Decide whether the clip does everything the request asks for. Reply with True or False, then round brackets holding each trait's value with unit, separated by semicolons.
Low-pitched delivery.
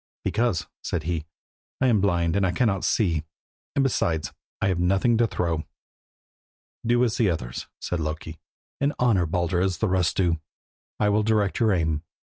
True (95 Hz)